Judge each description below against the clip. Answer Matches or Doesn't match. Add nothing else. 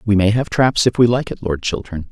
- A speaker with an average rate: Doesn't match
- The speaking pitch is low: Matches